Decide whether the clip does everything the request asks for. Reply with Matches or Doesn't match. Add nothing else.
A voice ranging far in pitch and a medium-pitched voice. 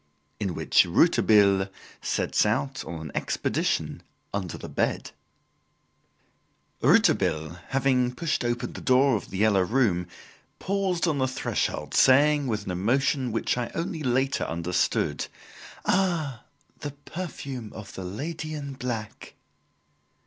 Doesn't match